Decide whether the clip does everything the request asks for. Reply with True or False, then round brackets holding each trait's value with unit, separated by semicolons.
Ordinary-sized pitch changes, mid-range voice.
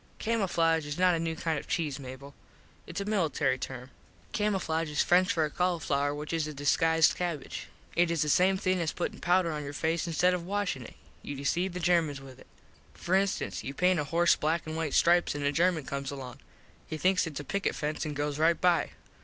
True (3.5 semitones; 165 Hz)